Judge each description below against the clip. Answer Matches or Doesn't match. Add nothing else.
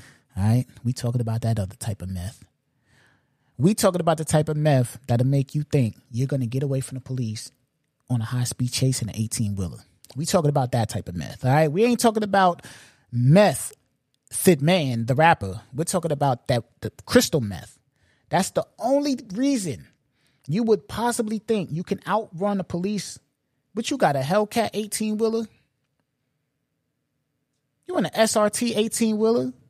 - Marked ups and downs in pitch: Matches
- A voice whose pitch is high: Doesn't match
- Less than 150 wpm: Doesn't match